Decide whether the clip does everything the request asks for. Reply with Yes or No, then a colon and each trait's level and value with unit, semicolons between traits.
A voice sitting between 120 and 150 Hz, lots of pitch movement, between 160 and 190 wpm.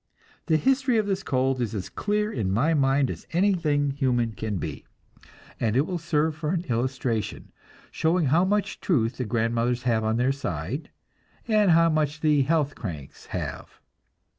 Yes: medium, 140 Hz; wide, 5.9 semitones; average, 165 wpm